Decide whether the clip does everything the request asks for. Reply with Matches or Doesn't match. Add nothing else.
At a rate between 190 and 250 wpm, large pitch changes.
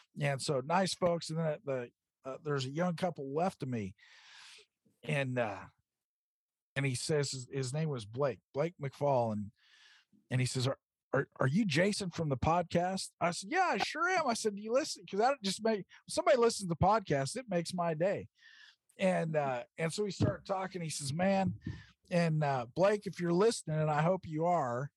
Matches